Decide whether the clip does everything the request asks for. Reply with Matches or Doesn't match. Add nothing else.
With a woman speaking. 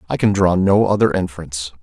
Doesn't match